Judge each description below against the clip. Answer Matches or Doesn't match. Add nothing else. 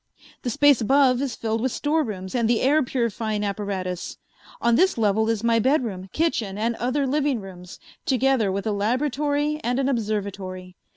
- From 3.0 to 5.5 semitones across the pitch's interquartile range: Matches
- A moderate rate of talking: Matches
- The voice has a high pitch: Matches